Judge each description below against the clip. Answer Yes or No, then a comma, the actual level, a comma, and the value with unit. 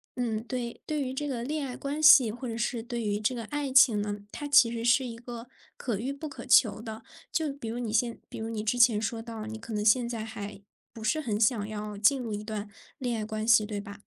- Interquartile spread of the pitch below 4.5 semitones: Yes, average, 2.8 semitones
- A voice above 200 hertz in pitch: Yes, high, 230 Hz